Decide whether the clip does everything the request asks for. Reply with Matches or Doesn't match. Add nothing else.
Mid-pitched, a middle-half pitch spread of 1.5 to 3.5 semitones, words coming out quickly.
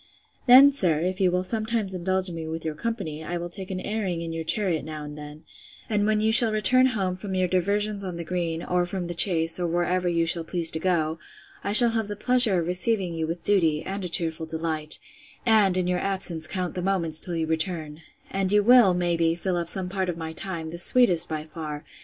Matches